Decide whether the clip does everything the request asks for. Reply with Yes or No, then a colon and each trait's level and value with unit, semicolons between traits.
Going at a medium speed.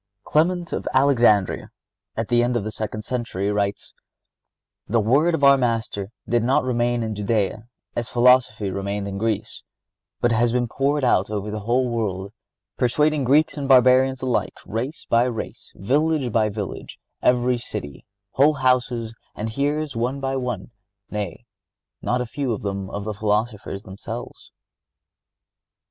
Yes: average, 145 wpm